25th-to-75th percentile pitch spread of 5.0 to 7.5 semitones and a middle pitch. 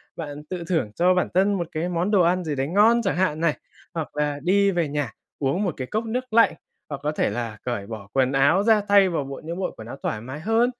Yes: wide, 5.5 semitones; medium, 170 Hz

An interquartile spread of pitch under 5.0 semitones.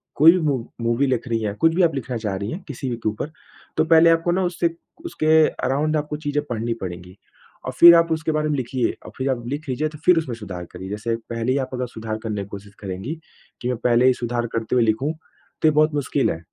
No: wide, 5.5 semitones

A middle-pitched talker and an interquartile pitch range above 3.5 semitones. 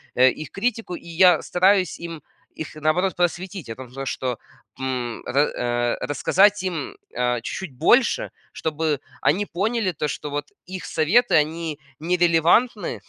Yes: medium, 165 Hz; average, 4.8 semitones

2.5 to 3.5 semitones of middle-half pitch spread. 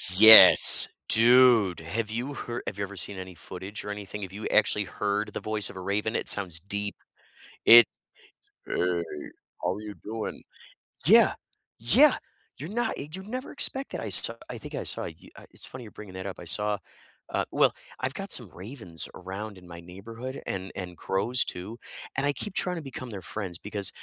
No: average, 3.9 semitones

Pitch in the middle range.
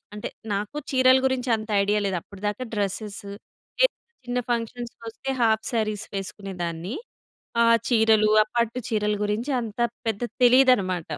No: high, 215 Hz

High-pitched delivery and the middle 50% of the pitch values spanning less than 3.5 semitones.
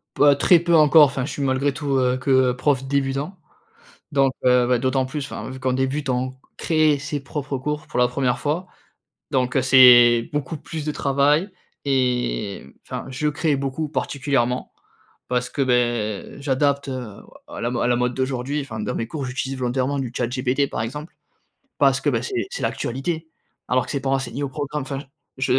No: low, 135 Hz; narrow, 2.5 semitones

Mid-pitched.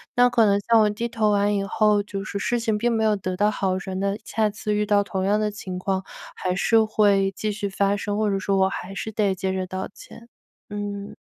No: high, 205 Hz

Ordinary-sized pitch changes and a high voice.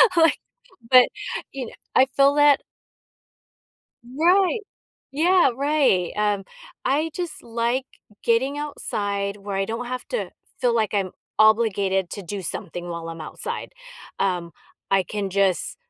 No: wide, 6.1 semitones; high, 225 Hz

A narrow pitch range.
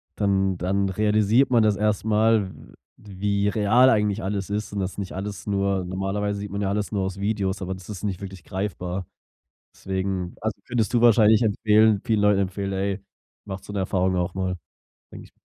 Yes: narrow, 1.8 semitones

